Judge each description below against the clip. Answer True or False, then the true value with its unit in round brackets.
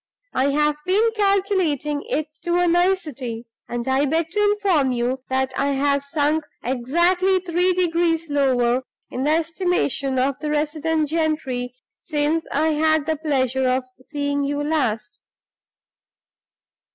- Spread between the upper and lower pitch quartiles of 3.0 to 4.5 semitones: True (3.9 semitones)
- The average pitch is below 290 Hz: False (300 Hz)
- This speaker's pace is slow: True (130 wpm)